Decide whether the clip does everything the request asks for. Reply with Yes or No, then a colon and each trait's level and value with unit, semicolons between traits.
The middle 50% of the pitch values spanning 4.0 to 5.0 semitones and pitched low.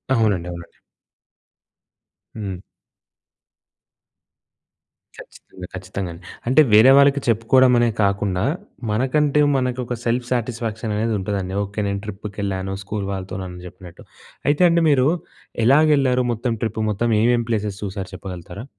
Yes: average, 4.4 semitones; low, 110 Hz